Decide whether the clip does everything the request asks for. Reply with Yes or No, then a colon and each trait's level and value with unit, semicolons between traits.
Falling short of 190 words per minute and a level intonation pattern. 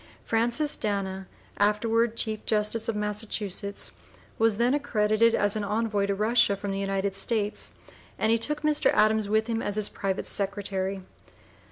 Yes: average, 155 wpm; narrow, 2.1 semitones